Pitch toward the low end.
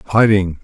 Yes: low, 100 Hz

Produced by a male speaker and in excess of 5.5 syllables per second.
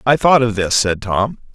No: male; 4.6 syllables/s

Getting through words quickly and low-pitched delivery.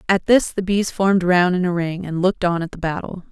No: fast, 270 wpm; medium, 180 Hz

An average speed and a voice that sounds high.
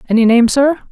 Yes: average, 195 wpm; very high, 250 Hz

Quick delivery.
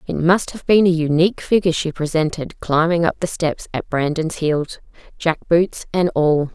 No: average, 185 wpm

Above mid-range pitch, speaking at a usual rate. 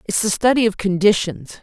Yes: high, 200 Hz; average, 185 wpm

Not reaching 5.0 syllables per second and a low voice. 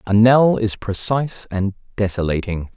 Yes: 4.6 syllables/s; low, 105 Hz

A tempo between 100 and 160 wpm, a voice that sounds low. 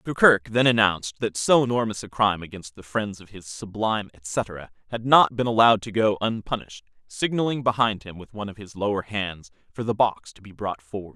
No: fast, 205 wpm; low, 105 Hz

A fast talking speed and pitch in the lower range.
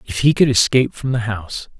Yes: fast, 235 wpm; low, 120 Hz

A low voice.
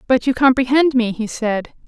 No: very high, 250 Hz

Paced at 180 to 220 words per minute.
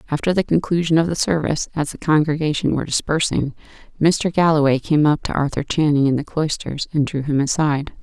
Yes: average, 185 wpm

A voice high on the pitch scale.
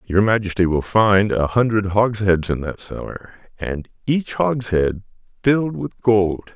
No: low, 105 Hz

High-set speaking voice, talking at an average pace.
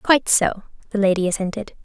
Yes: high, 205 Hz; average, 165 wpm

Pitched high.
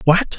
No: medium, 165 Hz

